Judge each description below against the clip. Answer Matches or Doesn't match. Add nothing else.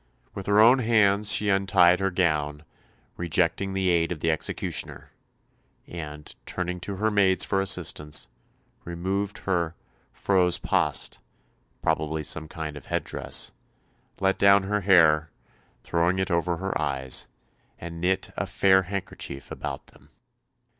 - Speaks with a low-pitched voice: Matches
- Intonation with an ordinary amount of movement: Matches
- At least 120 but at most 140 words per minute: Matches